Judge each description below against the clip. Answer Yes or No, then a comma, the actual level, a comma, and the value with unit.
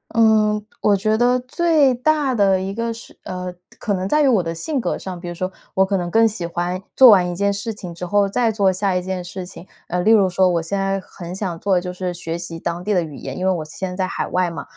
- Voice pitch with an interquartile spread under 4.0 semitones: Yes, average, 3.3 semitones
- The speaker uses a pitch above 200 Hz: No, high, 190 Hz